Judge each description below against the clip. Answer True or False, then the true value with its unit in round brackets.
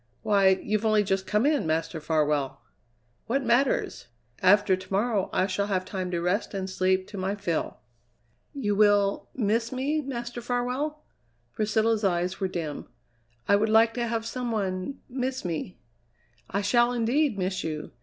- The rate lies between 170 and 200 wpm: False (160 wpm)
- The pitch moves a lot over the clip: False (4.3 semitones)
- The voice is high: True (205 Hz)